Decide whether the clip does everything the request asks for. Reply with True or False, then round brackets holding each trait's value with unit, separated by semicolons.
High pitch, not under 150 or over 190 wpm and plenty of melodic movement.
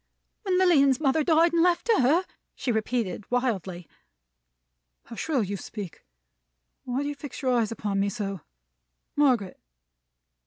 False (250 Hz; 140 wpm; 6.7 semitones)